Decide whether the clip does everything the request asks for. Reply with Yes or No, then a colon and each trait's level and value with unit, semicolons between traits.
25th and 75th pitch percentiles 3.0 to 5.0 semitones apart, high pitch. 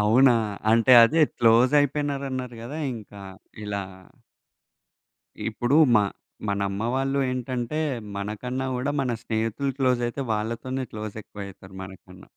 No: average, 3.9 semitones; low, 120 Hz